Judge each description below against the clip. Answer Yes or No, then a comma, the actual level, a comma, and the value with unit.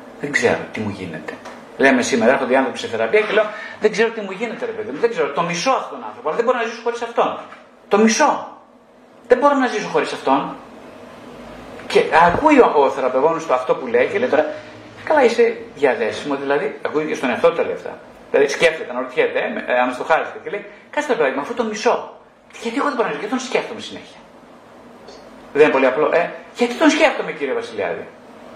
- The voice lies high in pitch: Yes, very high, 255 Hz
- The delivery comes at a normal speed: No, fast, 210 wpm